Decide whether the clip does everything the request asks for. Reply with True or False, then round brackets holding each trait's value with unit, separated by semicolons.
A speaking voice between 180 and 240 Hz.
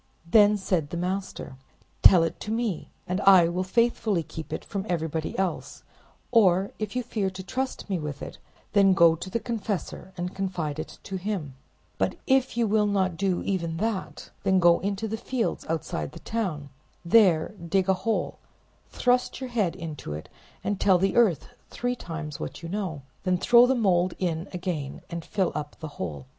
True (185 Hz)